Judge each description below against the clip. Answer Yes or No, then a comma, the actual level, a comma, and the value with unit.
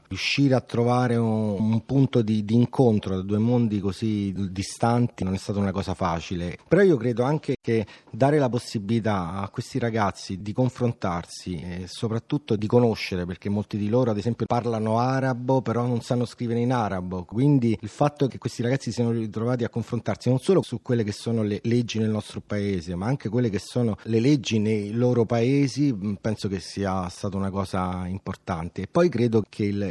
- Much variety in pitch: No, average, 3.4 semitones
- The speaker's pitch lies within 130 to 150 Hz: No, low, 115 Hz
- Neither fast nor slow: No, fast, 190 wpm